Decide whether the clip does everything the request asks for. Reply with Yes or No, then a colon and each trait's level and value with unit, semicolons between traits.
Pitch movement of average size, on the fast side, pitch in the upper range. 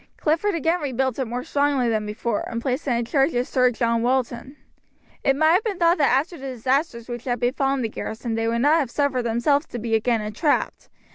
Yes: average, 3.5 semitones; fast, 220 wpm; very high, 255 Hz